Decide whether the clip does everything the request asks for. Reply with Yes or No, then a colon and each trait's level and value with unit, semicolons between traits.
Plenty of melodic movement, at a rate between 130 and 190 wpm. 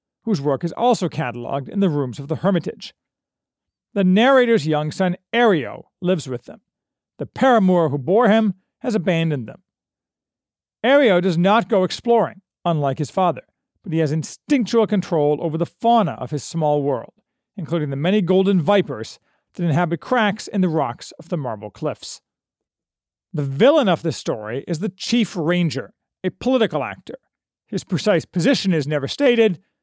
Yes: wide, 5.7 semitones; average, 160 wpm